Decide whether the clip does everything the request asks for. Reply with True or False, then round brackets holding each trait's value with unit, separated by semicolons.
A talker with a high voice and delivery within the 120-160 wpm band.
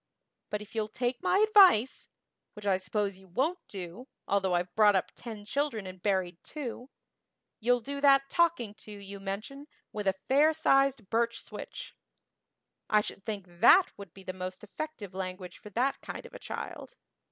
False (210 Hz; 175 wpm)